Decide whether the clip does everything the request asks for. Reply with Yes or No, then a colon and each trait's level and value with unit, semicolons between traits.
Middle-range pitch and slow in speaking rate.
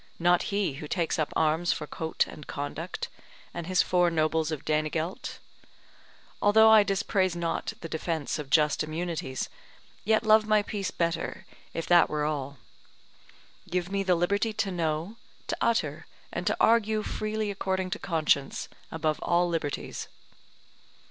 No: medium, 175 Hz; average, 150 wpm